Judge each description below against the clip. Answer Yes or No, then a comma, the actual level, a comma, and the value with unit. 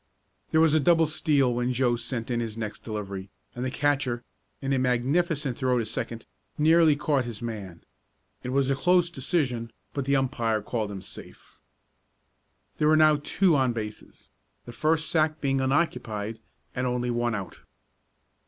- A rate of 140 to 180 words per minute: Yes, average, 165 wpm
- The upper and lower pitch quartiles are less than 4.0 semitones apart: No, average, 4.3 semitones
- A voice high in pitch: No, low, 130 Hz